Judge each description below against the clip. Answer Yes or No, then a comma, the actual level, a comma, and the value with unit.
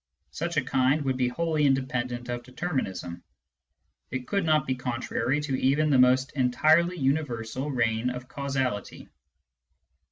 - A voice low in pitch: Yes, low, 130 Hz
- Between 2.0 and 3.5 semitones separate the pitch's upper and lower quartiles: Yes, average, 2.8 semitones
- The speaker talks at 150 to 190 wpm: No, slow, 135 wpm